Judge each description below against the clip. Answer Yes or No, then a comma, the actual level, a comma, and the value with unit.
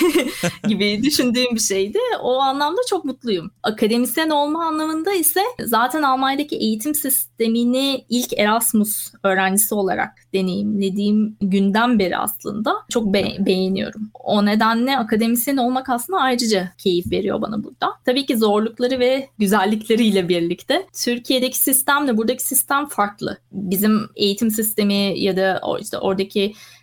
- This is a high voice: Yes, high, 225 Hz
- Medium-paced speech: Yes, average, 125 wpm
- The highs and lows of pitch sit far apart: No, average, 4.8 semitones